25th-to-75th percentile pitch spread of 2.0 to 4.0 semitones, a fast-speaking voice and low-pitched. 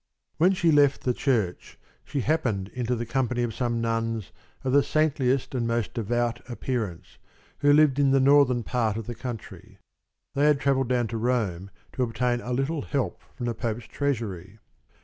No: average, 3.2 semitones; average, 175 wpm; low, 125 Hz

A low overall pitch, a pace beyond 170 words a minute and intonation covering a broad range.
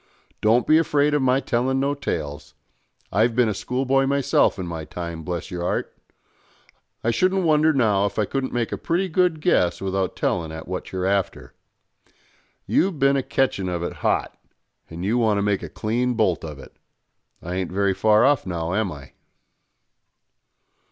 Yes: low, 110 Hz; average, 180 wpm; wide, 7.1 semitones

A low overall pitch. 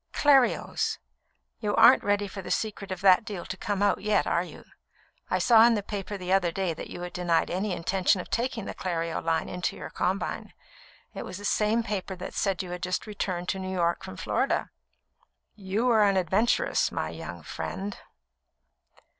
No: high, 195 Hz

